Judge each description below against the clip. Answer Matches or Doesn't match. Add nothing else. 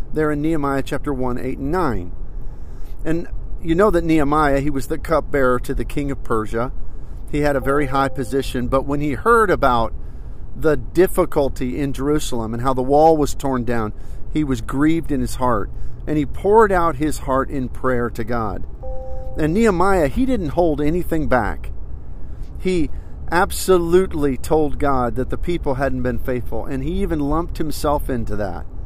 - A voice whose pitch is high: Doesn't match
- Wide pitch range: Doesn't match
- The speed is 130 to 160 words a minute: Doesn't match